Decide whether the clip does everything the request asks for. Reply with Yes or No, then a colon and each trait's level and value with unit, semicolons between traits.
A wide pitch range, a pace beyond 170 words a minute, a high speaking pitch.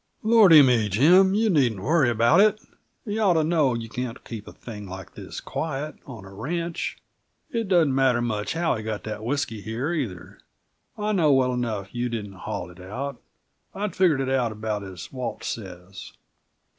No: wide, 7.1 semitones; average, 180 wpm; low, 125 Hz